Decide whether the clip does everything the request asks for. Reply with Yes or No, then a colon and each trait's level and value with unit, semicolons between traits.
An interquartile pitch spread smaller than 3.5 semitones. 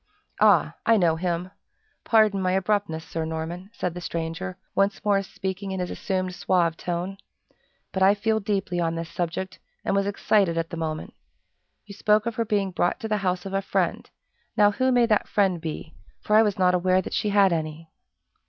Yes: average, 3.1 semitones